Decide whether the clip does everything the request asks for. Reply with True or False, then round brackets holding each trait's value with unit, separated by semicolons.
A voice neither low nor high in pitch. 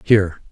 False (95 Hz)